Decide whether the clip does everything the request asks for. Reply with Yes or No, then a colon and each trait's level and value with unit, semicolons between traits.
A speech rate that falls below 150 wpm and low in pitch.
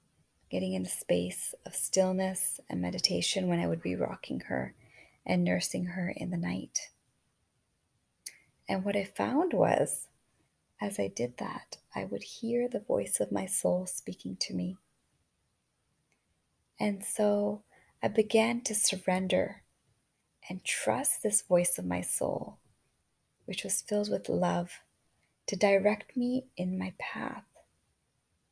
No: slow, 135 wpm; medium, 180 Hz